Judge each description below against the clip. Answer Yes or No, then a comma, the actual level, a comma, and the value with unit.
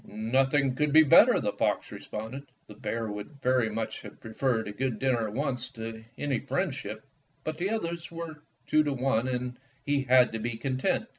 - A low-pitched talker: Yes, low, 130 Hz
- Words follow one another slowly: No, fast, 205 wpm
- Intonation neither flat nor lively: Yes, average, 4.2 semitones